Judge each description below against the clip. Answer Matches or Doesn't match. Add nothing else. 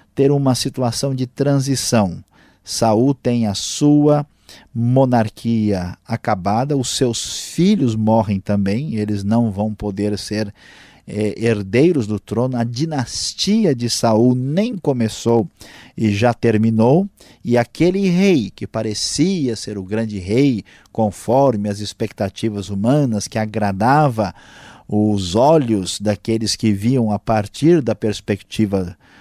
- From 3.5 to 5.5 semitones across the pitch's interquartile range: Matches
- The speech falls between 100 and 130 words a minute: Matches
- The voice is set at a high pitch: Doesn't match